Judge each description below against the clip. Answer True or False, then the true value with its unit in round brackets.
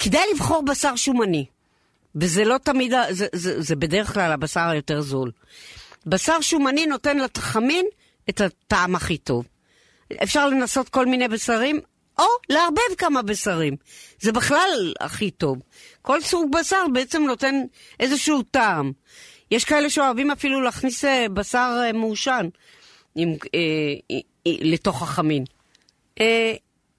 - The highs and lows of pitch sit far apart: True (8.7 semitones)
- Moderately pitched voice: False (240 Hz)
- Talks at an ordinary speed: True (125 wpm)